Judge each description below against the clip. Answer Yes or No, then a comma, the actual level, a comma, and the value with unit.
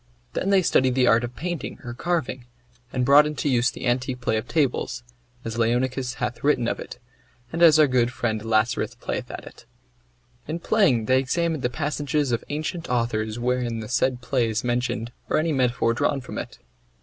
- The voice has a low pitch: Yes, low, 125 Hz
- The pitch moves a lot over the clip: No, average, 3.7 semitones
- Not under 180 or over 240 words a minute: Yes, average, 190 wpm